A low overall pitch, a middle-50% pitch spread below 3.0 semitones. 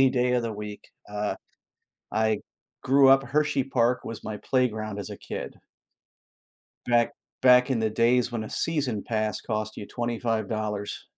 Yes: low, 115 Hz; narrow, 2.6 semitones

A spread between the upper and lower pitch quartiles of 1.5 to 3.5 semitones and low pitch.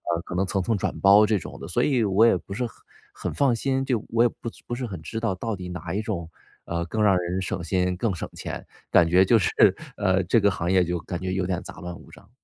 No: average, 4.0 semitones; very low, 95 Hz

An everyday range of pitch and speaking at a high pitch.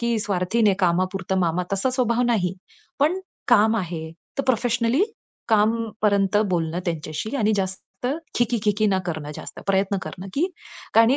Yes: average, 4.0 semitones; high, 205 Hz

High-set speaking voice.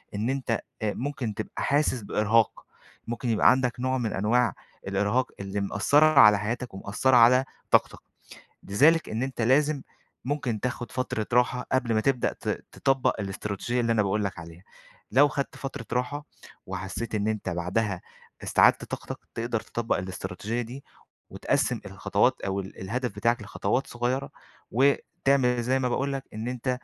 No: low, 120 Hz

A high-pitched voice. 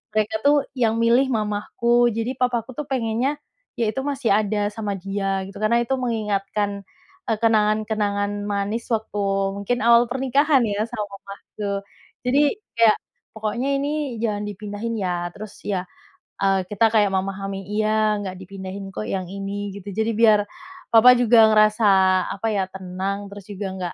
Yes: high, 215 Hz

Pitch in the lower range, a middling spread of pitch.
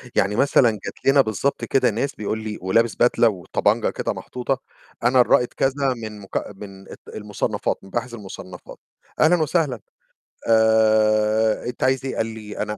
Yes: low, 110 Hz; average, 3.1 semitones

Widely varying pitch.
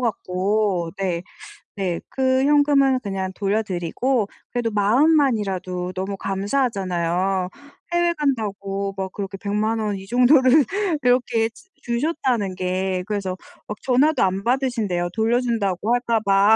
No: average, 4.6 semitones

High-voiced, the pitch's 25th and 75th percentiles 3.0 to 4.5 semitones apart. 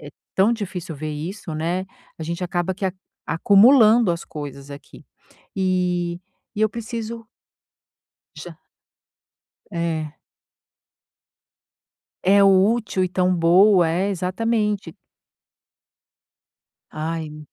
No: medium, 180 Hz; average, 3.8 semitones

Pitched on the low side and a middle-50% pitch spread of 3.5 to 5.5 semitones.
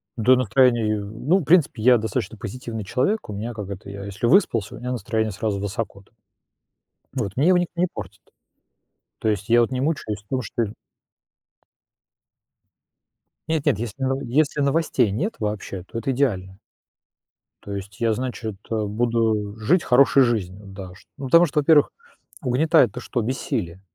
Yes: low, 115 Hz; average, 4.6 semitones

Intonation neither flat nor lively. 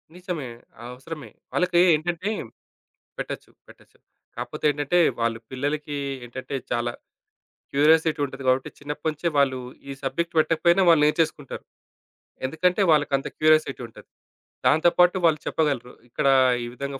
Yes: average, 3.3 semitones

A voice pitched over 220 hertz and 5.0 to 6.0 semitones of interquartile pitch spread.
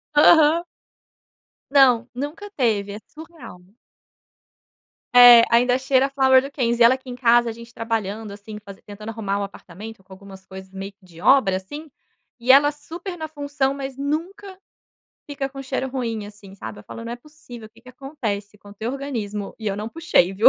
Yes: high, 240 Hz; average, 5.3 semitones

